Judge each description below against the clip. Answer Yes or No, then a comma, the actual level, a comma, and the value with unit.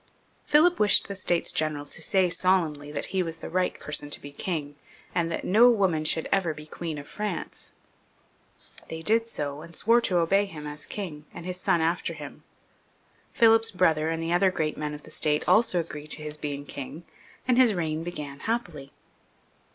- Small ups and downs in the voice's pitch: No, average, 4.1 semitones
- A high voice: No, medium, 165 Hz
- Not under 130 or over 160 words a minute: No, average, 190 wpm